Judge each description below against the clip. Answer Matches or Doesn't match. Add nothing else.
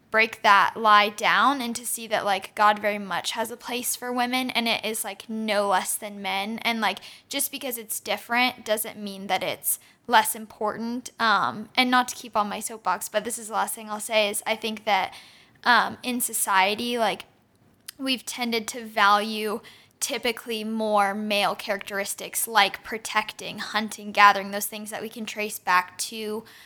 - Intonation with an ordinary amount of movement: Doesn't match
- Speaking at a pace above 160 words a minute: Matches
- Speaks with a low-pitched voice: Doesn't match